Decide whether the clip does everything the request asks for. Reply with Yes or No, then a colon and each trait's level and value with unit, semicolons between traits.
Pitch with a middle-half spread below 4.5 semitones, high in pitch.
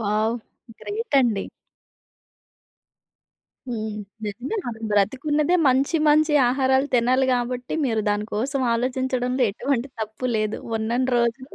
Yes: average, 3.2 semitones; very high, 250 Hz